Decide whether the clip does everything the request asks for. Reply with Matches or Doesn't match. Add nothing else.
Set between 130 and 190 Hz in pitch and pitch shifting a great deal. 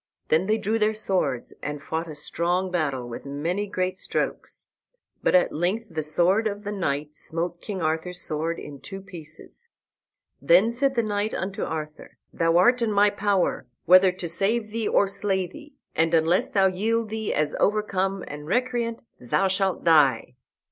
Doesn't match